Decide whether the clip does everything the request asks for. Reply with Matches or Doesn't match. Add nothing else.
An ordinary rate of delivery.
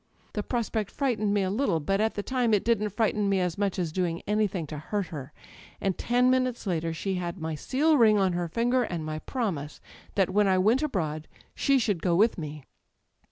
Doesn't match